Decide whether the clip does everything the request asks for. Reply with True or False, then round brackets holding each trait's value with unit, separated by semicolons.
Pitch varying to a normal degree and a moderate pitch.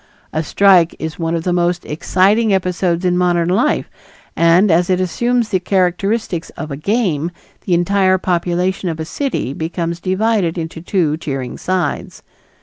False (2.3 semitones; 180 Hz)